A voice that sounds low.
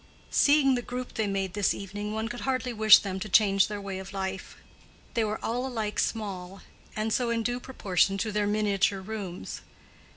No: high, 210 Hz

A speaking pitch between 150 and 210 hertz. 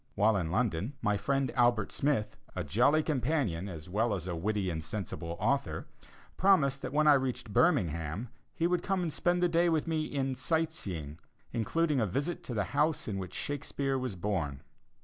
No: low, 125 Hz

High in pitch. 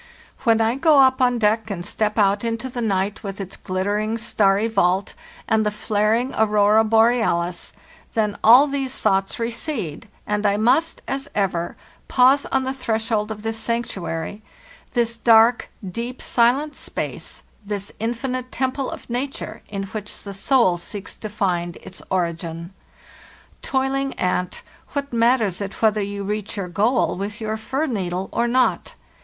Yes: high, 220 Hz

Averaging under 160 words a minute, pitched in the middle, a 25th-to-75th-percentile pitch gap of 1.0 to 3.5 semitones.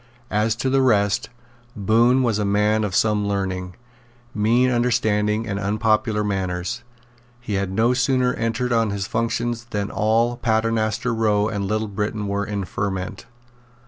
No: average, 150 wpm; low, 110 Hz; narrow, 2.4 semitones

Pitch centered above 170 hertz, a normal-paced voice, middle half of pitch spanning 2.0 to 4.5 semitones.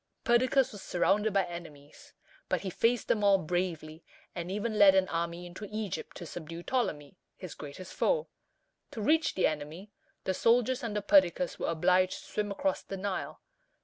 Yes: high, 190 Hz; average, 170 wpm; average, 3.8 semitones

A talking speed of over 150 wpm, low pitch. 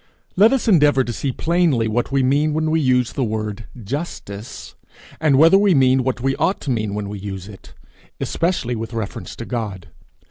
Yes: average, 190 wpm; low, 130 Hz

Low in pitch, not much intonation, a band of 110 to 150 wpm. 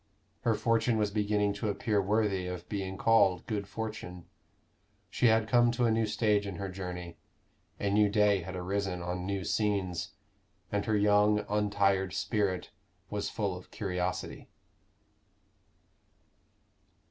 Yes: low, 100 Hz; narrow, 2.3 semitones; slow, 135 wpm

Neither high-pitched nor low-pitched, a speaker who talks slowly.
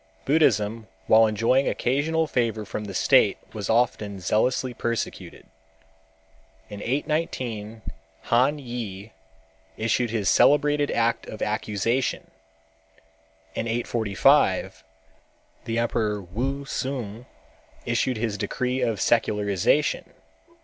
No: low, 115 Hz; slow, 95 wpm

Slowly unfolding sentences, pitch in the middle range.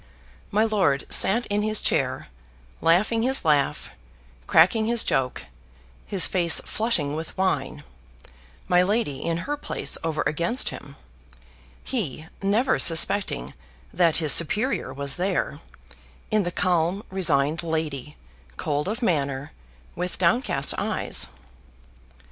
Yes: slow, 120 wpm; medium, 175 Hz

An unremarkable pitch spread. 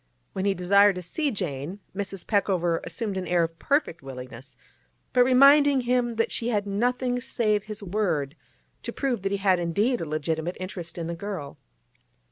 No: wide, 5.7 semitones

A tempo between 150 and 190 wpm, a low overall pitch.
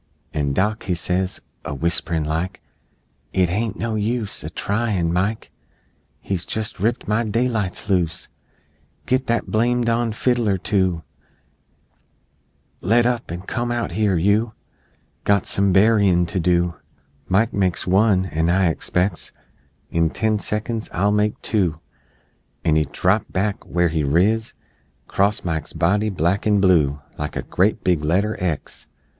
No: average, 140 wpm; very low, 95 Hz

